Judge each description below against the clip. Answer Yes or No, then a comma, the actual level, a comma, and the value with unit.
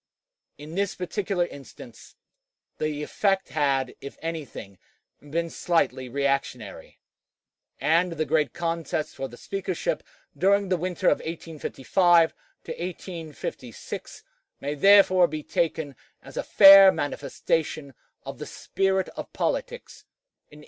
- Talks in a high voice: No, medium, 165 Hz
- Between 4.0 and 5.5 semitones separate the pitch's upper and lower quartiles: Yes, average, 4.3 semitones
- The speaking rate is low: Yes, slow, 115 wpm